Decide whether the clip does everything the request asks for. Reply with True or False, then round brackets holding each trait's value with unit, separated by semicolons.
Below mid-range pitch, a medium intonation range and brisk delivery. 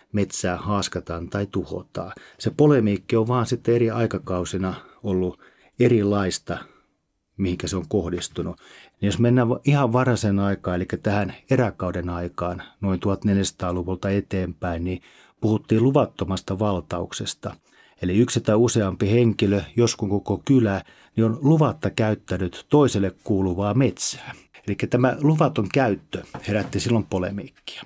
False (100 Hz; 4.1 semitones; 120 wpm)